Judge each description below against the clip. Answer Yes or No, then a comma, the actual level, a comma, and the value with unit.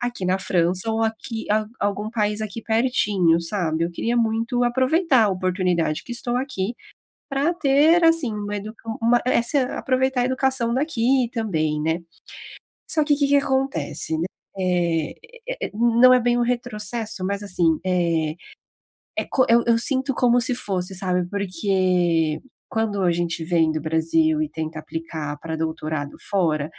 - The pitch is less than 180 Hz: No, high, 210 Hz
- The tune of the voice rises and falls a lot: Yes, wide, 6.3 semitones